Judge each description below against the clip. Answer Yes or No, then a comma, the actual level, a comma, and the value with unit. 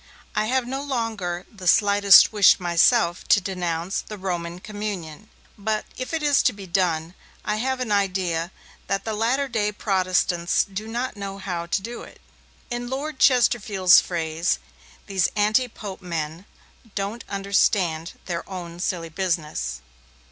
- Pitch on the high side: Yes, high, 195 Hz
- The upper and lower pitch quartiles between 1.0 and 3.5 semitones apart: No, average, 3.9 semitones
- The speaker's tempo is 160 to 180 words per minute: No, average, 150 wpm